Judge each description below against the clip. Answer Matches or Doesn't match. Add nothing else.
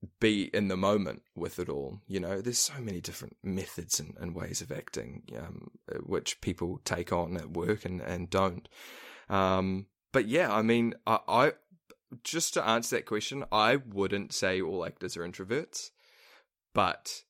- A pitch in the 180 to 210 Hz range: Doesn't match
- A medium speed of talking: Matches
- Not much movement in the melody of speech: Doesn't match